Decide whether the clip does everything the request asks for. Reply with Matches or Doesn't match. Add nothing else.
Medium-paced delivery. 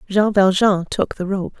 Matches